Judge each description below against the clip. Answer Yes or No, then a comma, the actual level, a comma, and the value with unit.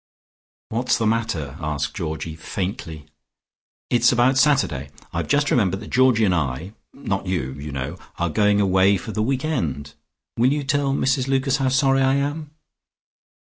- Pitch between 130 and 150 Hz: No, low, 110 Hz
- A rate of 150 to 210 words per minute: Yes, average, 155 wpm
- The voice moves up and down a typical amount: No, wide, 8.6 semitones